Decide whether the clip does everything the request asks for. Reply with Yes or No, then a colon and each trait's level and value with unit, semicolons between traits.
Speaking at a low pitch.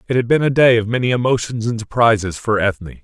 Yes: low, 115 Hz